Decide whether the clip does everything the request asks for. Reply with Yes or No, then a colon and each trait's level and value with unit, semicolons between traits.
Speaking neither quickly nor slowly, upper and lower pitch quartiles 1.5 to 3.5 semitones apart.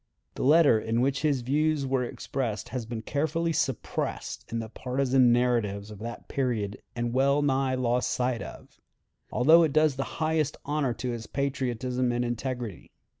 Yes: average, 160 wpm; average, 2.8 semitones